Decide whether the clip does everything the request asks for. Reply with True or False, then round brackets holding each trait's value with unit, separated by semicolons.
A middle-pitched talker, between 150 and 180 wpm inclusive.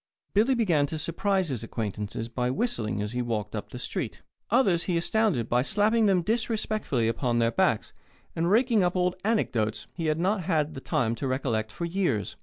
False (160 Hz; 190 wpm)